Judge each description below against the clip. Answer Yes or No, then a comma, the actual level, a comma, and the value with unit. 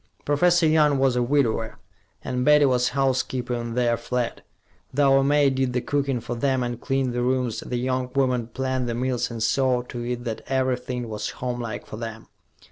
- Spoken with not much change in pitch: Yes, narrow, 1.9 semitones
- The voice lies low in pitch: Yes, low, 125 Hz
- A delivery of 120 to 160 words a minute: No, average, 190 wpm